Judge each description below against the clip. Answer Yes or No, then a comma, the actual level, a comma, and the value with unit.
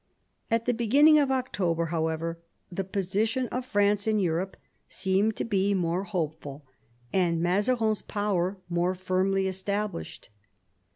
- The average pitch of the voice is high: Yes, high, 195 Hz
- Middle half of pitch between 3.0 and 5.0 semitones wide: Yes, average, 3.7 semitones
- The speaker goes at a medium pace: No, slow, 125 wpm